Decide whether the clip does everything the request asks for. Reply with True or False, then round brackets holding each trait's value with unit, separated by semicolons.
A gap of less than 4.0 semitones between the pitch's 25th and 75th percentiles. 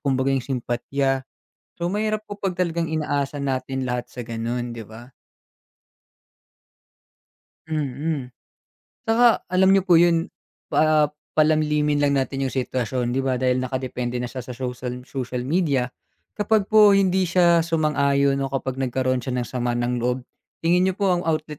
False (4.7 semitones)